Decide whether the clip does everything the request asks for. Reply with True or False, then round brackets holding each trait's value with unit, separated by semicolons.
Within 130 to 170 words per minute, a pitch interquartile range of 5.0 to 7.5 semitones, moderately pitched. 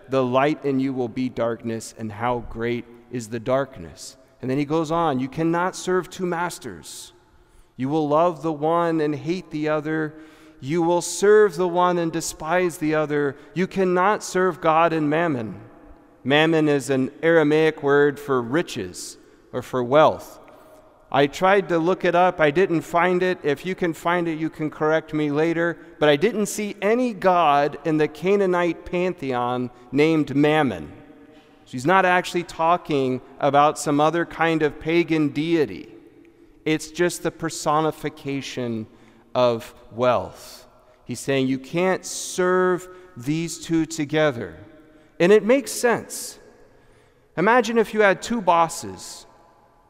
False (150 wpm; 4.2 semitones; 155 Hz)